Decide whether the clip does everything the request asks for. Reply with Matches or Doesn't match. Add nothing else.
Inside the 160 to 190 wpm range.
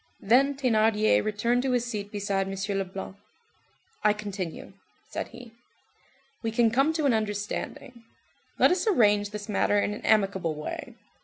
Doesn't match